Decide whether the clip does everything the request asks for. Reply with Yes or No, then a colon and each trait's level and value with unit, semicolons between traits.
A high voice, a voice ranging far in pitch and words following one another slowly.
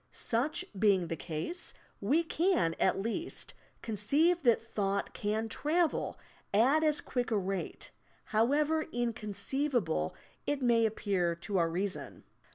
Yes: high, 225 Hz; wide, 6.9 semitones; slow, 125 wpm